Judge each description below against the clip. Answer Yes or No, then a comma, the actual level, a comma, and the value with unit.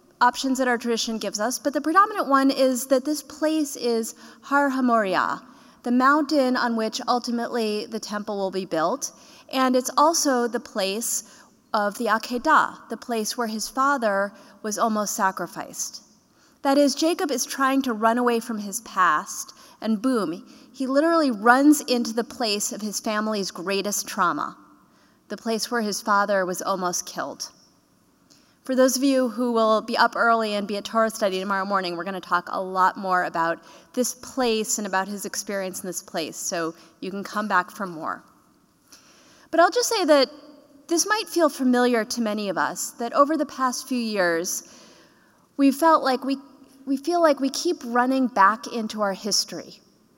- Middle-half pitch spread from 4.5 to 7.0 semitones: Yes, average, 4.8 semitones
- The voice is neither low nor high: No, high, 235 Hz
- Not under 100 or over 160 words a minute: No, average, 175 wpm